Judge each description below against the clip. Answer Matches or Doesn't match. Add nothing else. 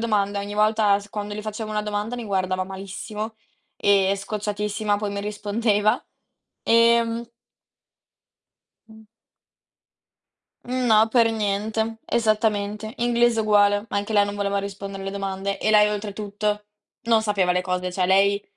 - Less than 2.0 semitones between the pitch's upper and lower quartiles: Matches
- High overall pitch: Matches